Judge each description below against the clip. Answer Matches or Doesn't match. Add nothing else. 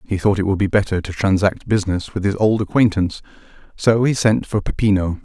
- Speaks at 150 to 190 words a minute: Doesn't match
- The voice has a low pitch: Matches